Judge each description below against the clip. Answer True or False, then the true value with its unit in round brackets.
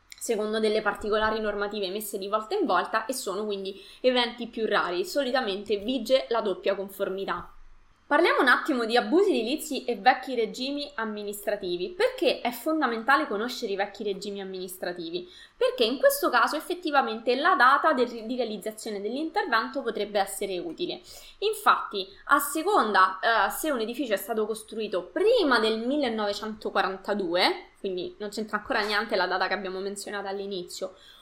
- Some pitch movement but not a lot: False (5.7 semitones)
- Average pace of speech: True (145 wpm)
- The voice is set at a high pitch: True (225 Hz)